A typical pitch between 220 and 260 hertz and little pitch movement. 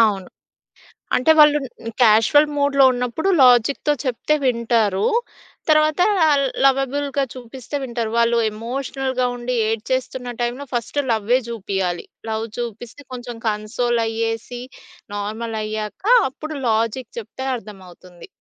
No: high, 240 Hz; average, 3.2 semitones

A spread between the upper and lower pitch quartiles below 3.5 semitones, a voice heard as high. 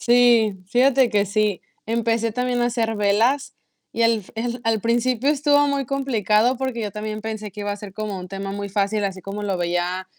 Yes: average, 3.1 semitones; high, 220 Hz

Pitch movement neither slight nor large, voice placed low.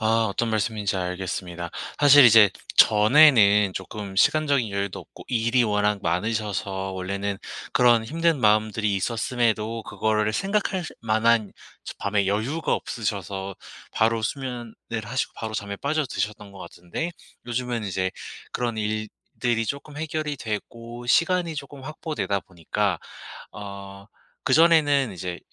Yes: average, 4.0 semitones; low, 110 Hz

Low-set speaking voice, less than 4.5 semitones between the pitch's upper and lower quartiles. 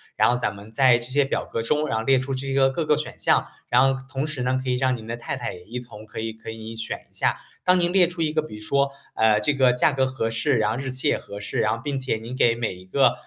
Yes: low, 125 Hz; average, 3.5 semitones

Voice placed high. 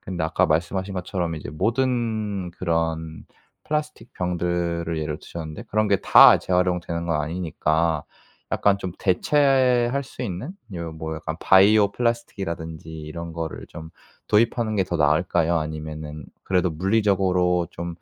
No: very low, 90 Hz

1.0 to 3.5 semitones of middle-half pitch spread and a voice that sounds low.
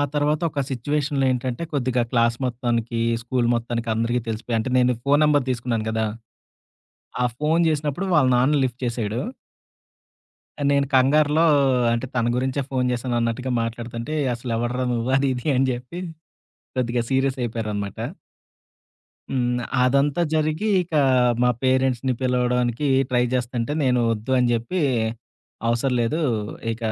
Yes: average, 2.8 semitones; low, 125 Hz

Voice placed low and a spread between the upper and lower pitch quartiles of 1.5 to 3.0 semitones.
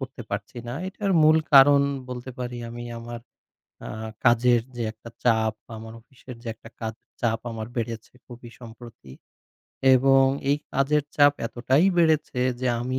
Yes: low, 120 Hz; average, 2.7 semitones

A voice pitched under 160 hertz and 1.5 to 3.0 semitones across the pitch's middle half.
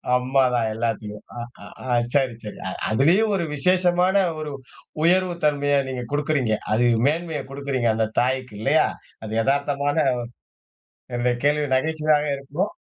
No: medium, 140 Hz; average, 4.1 semitones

